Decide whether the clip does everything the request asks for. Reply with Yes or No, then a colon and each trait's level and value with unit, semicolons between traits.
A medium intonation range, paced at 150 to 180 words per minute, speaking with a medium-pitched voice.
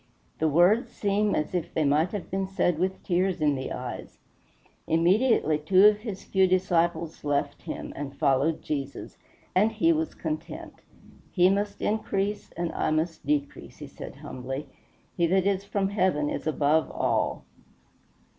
Yes: average, 4.6 semitones; average, 155 wpm; medium, 180 Hz